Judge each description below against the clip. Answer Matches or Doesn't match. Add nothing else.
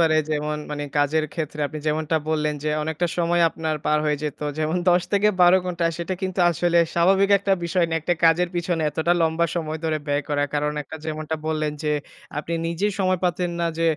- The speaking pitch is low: Doesn't match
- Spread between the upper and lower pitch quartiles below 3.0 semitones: Matches